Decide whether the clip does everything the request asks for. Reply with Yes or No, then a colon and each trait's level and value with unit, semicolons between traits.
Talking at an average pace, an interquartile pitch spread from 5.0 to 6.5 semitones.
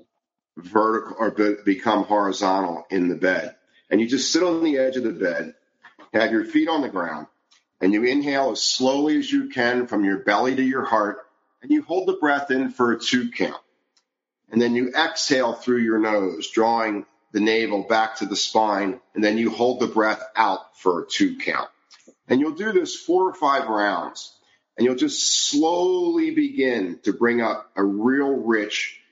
Yes: average, 190 wpm; wide, 5.5 semitones